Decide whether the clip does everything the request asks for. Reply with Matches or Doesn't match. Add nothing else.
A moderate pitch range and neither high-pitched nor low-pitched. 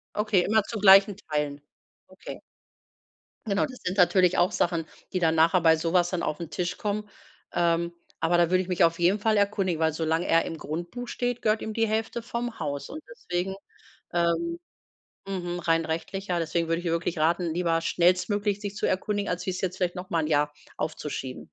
Matches